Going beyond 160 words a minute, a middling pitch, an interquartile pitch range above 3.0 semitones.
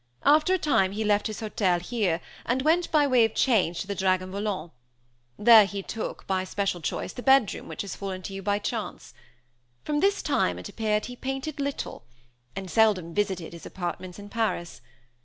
No: average, 190 wpm; high, 205 Hz; average, 4.8 semitones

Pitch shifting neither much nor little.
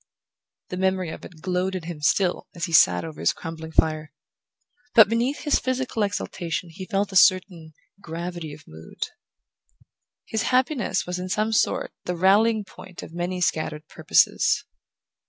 Yes: average, 3.8 semitones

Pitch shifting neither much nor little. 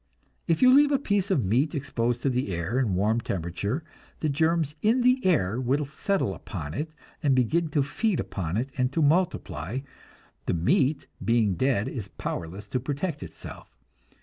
No: wide, 7.8 semitones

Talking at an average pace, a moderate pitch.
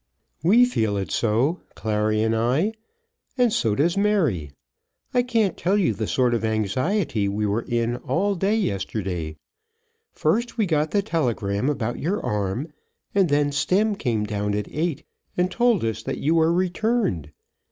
Yes: average, 160 wpm; medium, 145 Hz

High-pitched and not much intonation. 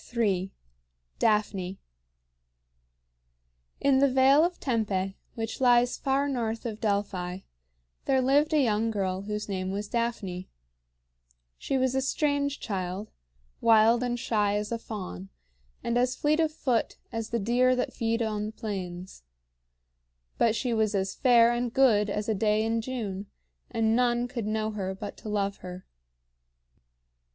No: high, 225 Hz; average, 3.5 semitones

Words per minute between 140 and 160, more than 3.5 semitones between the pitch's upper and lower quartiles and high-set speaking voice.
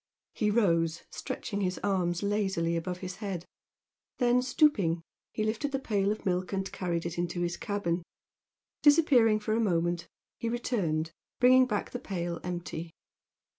Yes: average, 150 wpm; average, 4.4 semitones; high, 195 Hz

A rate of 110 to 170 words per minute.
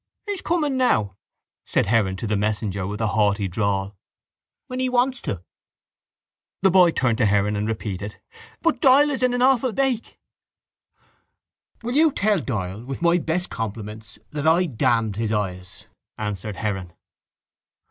Yes: average, 150 wpm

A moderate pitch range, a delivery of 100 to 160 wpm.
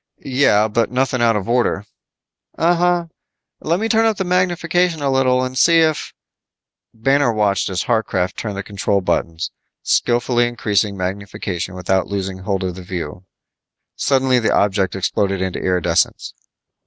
No: wide, 6.0 semitones; average, 150 wpm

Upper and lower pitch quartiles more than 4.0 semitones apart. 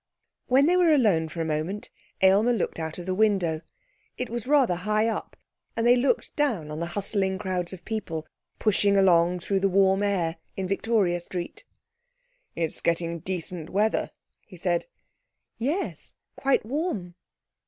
Yes: average, 4.5 semitones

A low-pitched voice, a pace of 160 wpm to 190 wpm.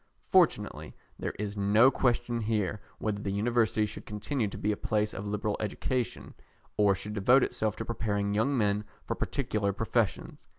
Yes: low, 105 Hz; average, 165 wpm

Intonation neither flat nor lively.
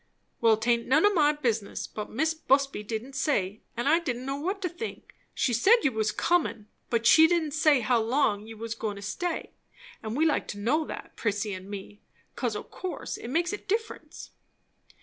No: wide, 6.6 semitones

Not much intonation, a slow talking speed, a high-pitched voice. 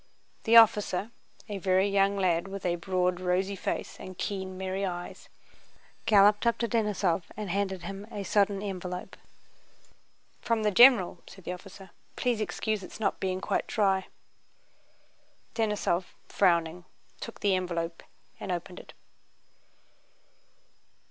Yes: narrow, 2.3 semitones; slow, 130 wpm; high, 195 Hz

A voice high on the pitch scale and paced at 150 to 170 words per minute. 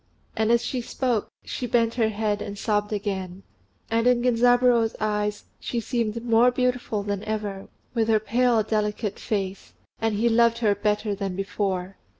Yes: high, 220 Hz; average, 160 wpm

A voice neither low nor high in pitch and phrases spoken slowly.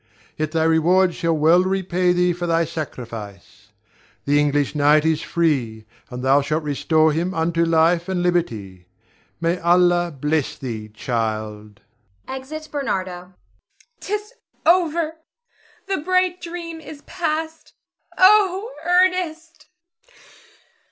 Yes: medium, 170 Hz; slow, 120 wpm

